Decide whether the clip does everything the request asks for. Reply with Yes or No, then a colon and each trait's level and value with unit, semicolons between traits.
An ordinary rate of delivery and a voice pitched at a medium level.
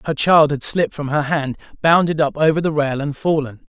No: fast, 225 wpm; medium, 150 Hz